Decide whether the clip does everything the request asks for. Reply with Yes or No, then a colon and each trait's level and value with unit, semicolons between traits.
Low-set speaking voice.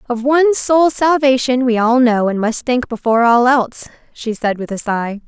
No: high, 245 Hz